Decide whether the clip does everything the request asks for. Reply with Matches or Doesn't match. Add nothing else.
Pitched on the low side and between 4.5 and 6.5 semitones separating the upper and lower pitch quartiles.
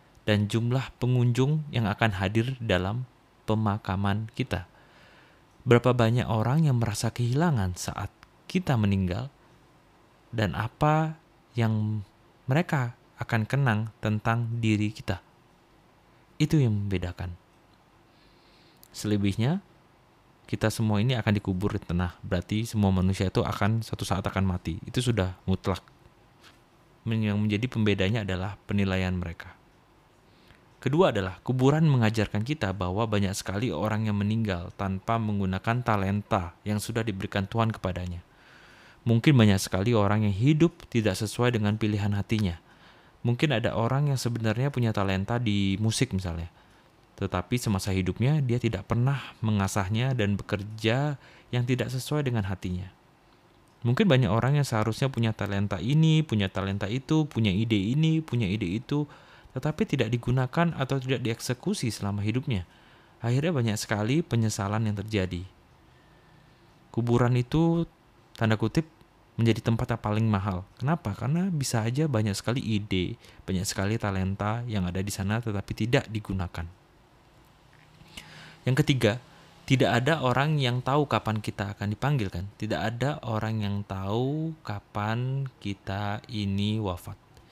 Doesn't match